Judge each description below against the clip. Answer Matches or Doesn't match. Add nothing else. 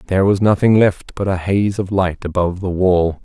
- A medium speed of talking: Doesn't match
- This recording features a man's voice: Matches